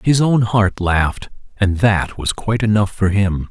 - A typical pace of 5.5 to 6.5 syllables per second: No, 4.4 syllables/s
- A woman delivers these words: No, male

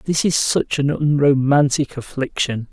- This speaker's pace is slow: Yes, slow, 130 wpm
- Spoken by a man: Yes, male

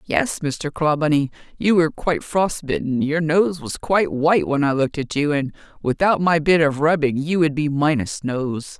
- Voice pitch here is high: No, medium, 155 Hz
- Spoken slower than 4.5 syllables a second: No, 4.9 syllables/s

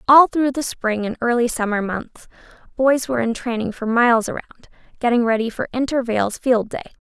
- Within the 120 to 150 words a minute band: No, average, 180 wpm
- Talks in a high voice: Yes, high, 240 Hz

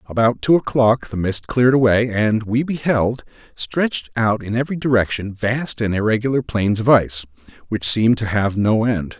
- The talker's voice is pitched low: Yes, low, 115 Hz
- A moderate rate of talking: Yes, average, 175 wpm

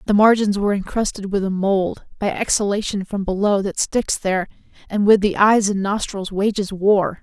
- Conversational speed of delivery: Yes, average, 185 wpm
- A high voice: Yes, high, 200 Hz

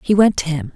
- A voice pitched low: No, medium, 175 Hz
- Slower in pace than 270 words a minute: No, fast, 320 wpm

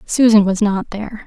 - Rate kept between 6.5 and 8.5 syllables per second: No, 5.1 syllables/s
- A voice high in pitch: Yes, high, 210 Hz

